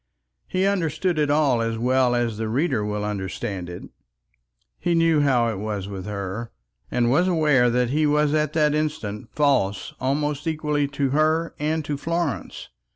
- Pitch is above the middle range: No, medium, 140 Hz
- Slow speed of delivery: No, average, 165 wpm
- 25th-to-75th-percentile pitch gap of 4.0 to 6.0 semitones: Yes, average, 5.3 semitones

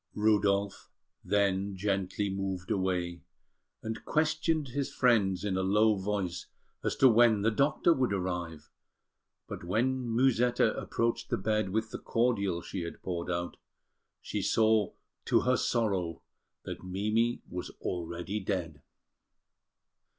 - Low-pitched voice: Yes, low, 100 Hz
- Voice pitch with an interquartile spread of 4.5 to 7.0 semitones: No, average, 3.7 semitones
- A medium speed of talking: No, slow, 130 wpm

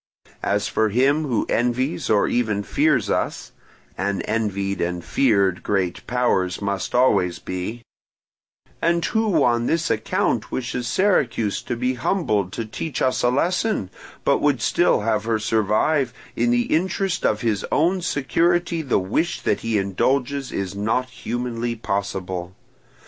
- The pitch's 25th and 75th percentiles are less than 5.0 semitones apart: No, wide, 5.6 semitones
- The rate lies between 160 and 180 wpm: No, average, 145 wpm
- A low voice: Yes, low, 120 Hz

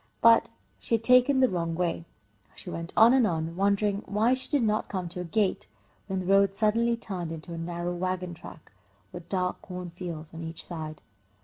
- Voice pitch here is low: No, medium, 185 Hz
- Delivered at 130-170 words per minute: No, average, 200 wpm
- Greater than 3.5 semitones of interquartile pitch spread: Yes, average, 4.1 semitones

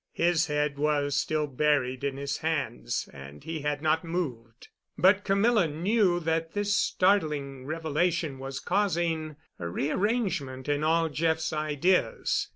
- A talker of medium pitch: Yes, medium, 155 Hz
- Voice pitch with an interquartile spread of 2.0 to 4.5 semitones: Yes, average, 3.6 semitones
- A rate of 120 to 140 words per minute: Yes, slow, 135 wpm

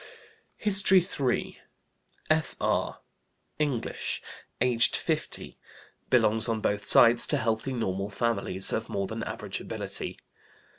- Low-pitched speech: Yes, low, 115 Hz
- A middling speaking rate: No, slow, 105 wpm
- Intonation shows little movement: No, average, 3.4 semitones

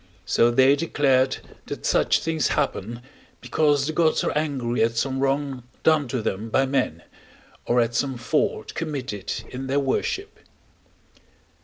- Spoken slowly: No, average, 145 wpm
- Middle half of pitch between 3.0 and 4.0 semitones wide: Yes, average, 3.4 semitones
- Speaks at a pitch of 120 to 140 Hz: Yes, low, 135 Hz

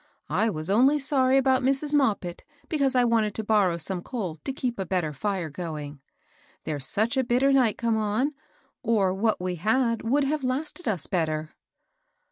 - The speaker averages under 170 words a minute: No, average, 175 wpm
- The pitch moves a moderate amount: No, wide, 6.5 semitones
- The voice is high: Yes, high, 220 Hz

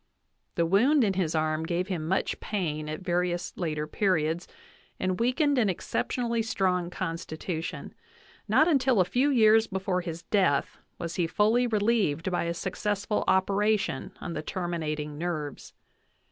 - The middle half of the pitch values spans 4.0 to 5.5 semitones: Yes, average, 4.3 semitones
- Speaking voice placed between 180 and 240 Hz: Yes, medium, 185 Hz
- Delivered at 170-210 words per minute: No, average, 145 wpm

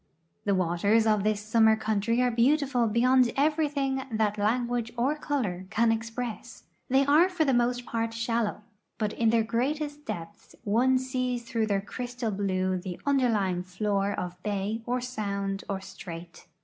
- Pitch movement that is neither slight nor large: Yes, average, 3.7 semitones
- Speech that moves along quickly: No, average, 155 wpm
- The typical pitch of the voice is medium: No, high, 230 Hz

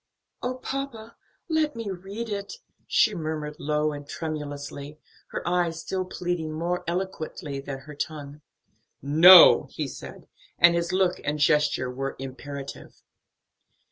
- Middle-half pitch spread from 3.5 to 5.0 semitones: Yes, average, 4.4 semitones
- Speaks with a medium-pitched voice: Yes, medium, 160 Hz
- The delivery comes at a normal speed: No, slow, 130 wpm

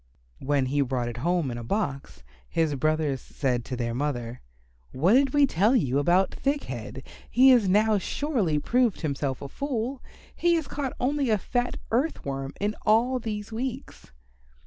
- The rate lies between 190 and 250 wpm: No, average, 170 wpm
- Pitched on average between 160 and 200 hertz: Yes, medium, 185 Hz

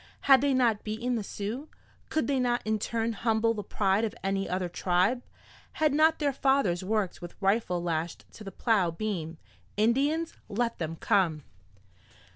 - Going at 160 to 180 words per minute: Yes, average, 165 wpm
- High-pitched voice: Yes, high, 215 Hz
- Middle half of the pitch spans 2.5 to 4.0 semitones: No, average, 4.9 semitones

